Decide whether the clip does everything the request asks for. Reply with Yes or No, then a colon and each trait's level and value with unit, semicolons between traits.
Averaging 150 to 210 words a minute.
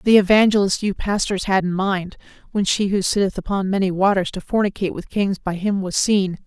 Yes: fast, 205 wpm